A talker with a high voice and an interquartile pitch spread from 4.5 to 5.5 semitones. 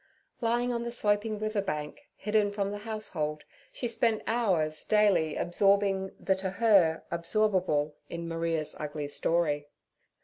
Yes: high, 195 Hz; average, 4.9 semitones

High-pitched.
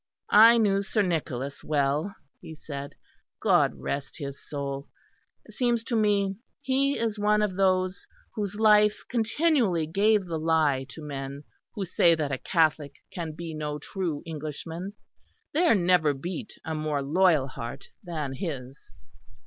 No: medium, 170 Hz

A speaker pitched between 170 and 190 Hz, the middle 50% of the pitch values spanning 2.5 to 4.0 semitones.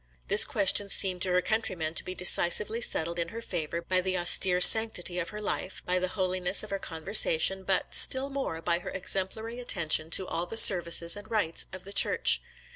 Yes: medium, 185 Hz; average, 3.1 semitones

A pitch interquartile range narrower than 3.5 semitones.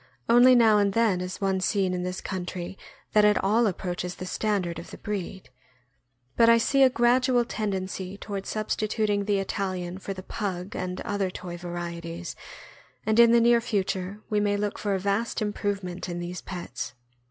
Yes: average, 2.9 semitones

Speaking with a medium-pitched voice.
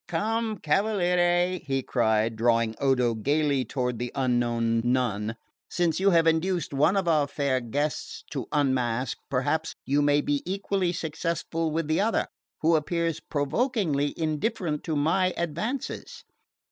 Yes: medium, 150 Hz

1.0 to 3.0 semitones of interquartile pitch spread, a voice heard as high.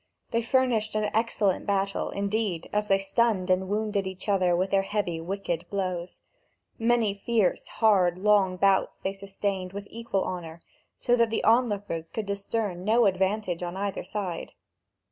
Yes: narrow, 2.6 semitones; high, 200 Hz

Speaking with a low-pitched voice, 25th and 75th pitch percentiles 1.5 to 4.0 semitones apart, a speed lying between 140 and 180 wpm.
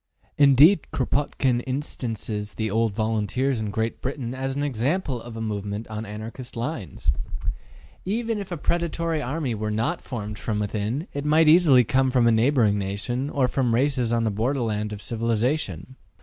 No: low, 120 Hz; average, 4.6 semitones; average, 165 wpm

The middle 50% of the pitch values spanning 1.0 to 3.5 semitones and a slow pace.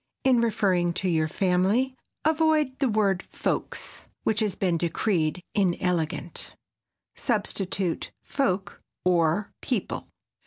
No: average, 4.5 semitones; slow, 105 wpm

